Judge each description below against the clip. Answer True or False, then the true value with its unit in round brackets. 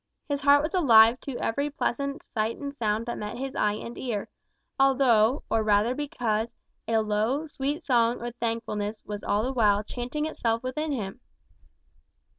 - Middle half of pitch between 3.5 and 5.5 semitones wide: True (4.3 semitones)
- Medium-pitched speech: False (235 Hz)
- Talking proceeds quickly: False (165 wpm)